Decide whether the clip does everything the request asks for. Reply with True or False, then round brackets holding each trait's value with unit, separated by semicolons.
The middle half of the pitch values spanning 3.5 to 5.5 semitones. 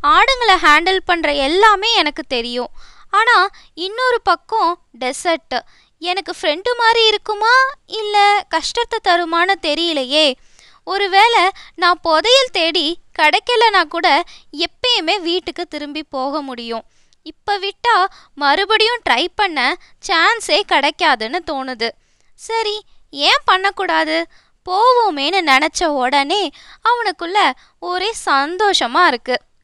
True (5.1 semitones)